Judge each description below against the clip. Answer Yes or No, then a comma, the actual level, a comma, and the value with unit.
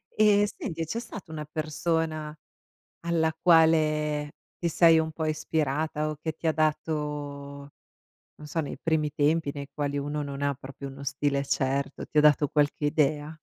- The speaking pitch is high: No, medium, 150 Hz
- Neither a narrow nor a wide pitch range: No, narrow, 1.7 semitones